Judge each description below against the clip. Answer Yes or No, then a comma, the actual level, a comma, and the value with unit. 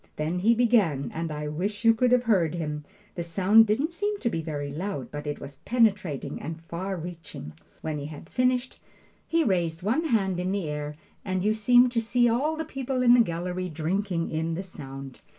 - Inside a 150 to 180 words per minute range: No, fast, 205 wpm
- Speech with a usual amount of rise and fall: No, wide, 6.6 semitones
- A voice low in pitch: No, medium, 185 Hz